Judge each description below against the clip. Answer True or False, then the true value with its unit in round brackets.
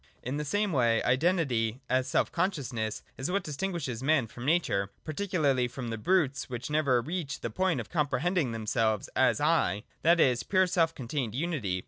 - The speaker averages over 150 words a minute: True (175 wpm)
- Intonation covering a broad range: True (6.0 semitones)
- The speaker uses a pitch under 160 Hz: True (140 Hz)